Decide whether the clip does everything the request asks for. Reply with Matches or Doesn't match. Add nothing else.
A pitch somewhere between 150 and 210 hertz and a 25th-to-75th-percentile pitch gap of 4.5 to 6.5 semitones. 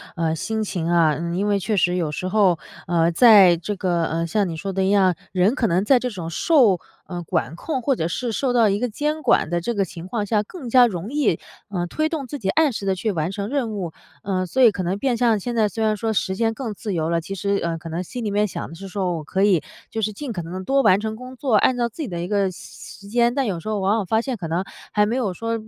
Matches